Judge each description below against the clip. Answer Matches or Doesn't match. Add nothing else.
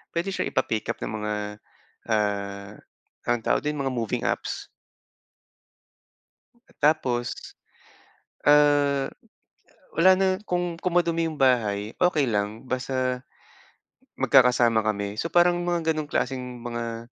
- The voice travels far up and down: Matches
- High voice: Doesn't match